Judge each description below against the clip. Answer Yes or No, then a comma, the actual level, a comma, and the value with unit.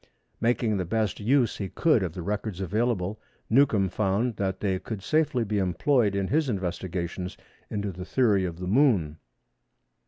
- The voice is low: Yes, low, 100 Hz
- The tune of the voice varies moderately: Yes, average, 4.0 semitones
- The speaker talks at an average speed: Yes, average, 160 wpm